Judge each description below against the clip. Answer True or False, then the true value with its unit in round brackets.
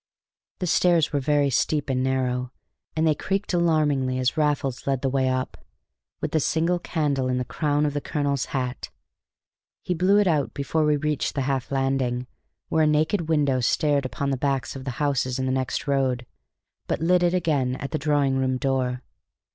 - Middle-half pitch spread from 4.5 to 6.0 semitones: False (3.0 semitones)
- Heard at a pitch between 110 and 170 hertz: True (140 Hz)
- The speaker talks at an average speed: True (190 wpm)